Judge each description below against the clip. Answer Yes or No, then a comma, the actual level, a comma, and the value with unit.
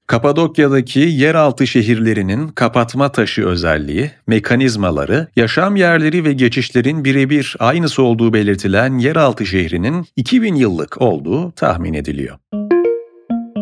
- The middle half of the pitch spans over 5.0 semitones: Yes, wide, 5.4 semitones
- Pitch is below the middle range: Yes, low, 130 Hz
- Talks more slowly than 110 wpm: Yes, slow, 95 wpm